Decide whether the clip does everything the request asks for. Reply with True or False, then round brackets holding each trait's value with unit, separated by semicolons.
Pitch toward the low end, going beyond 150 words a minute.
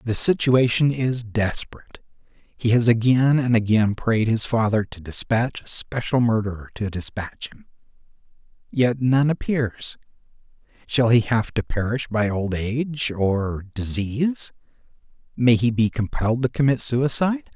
False (120 Hz; 135 wpm)